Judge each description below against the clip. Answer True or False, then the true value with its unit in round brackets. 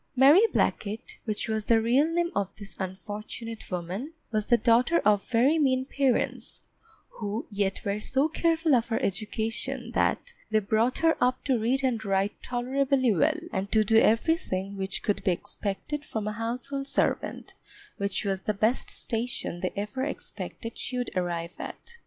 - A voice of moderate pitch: False (230 Hz)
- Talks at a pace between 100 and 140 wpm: False (165 wpm)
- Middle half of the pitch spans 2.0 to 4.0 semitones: False (4.6 semitones)